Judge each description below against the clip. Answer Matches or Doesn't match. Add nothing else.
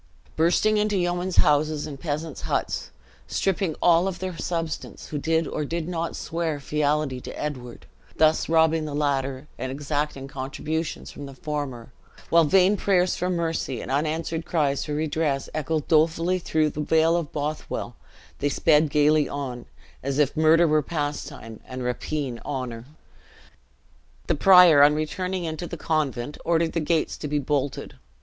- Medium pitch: Matches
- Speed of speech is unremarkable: Matches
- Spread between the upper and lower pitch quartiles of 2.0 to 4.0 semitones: Matches